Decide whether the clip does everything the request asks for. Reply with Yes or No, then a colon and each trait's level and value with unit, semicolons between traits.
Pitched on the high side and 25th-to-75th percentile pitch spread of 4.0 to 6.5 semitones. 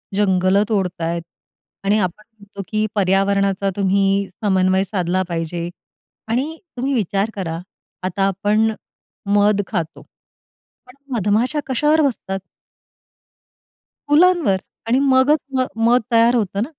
No: high, 200 Hz; average, 3.6 semitones